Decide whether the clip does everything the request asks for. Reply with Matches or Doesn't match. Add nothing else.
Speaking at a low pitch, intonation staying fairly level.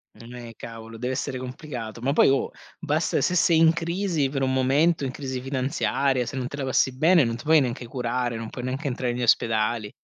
Doesn't match